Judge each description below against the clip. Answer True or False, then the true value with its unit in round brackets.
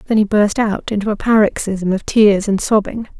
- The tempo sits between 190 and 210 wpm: True (205 wpm)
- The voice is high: True (205 Hz)